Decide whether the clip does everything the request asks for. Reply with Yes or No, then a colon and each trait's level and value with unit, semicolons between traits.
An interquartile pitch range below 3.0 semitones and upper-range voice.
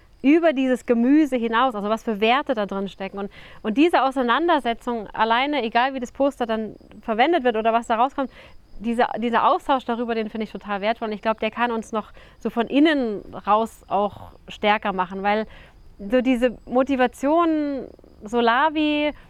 No: average, 3.3 semitones; high, 235 Hz